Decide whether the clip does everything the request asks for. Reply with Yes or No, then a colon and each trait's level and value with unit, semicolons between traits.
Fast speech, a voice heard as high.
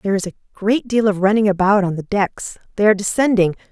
Yes: fast, 210 wpm; high, 200 Hz